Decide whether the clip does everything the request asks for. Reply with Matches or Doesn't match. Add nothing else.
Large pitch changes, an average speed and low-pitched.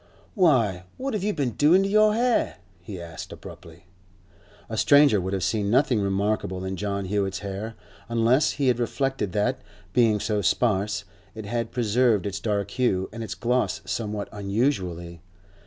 Doesn't match